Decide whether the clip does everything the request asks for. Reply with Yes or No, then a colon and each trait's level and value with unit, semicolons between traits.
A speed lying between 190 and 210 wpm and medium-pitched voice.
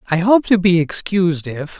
Yes: average, 200 wpm; medium, 180 Hz